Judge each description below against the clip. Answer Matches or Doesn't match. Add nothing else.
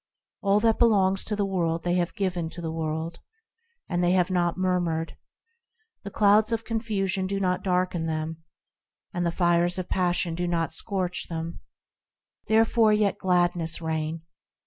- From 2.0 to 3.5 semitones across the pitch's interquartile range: Matches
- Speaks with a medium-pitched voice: Matches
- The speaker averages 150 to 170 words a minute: Matches